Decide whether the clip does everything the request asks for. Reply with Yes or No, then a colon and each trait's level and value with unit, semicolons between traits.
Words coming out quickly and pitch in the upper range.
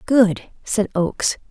No: slow, 120 wpm; high, 210 Hz